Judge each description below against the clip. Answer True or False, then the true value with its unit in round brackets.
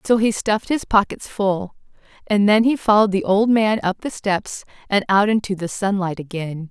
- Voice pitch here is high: True (205 Hz)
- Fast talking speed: False (195 wpm)